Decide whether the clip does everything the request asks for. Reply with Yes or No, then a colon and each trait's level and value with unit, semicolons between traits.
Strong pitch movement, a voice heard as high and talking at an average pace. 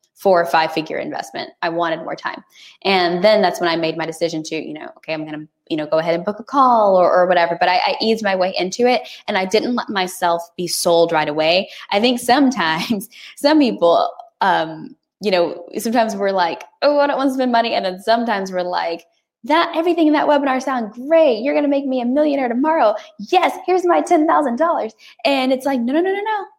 No: wide, 8.7 semitones; high, 225 Hz; fast, 230 wpm